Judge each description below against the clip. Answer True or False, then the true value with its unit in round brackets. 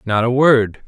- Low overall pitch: True (120 Hz)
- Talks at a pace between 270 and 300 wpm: False (205 wpm)